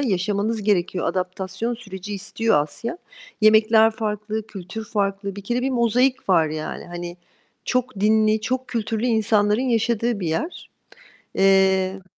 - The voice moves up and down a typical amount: Yes, average, 3.1 semitones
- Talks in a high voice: Yes, high, 210 Hz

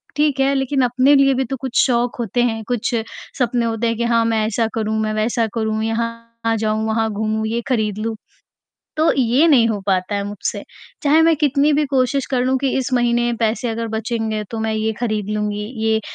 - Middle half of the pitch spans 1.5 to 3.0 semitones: Yes, average, 2.7 semitones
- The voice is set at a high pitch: Yes, high, 230 Hz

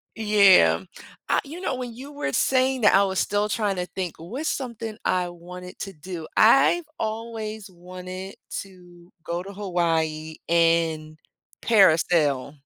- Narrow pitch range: No, average, 4.4 semitones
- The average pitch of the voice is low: No, medium, 185 Hz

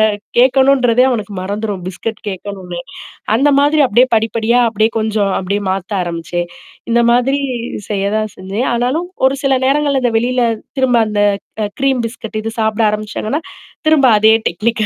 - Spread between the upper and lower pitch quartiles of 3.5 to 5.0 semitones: Yes, average, 3.9 semitones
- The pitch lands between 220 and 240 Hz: Yes, high, 225 Hz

